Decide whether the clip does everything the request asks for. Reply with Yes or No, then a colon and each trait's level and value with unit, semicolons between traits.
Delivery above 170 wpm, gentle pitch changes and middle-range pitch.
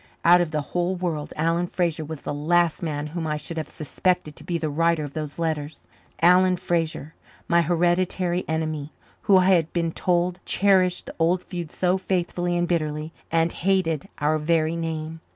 Yes: average, 180 wpm; narrow, 2.1 semitones; medium, 170 Hz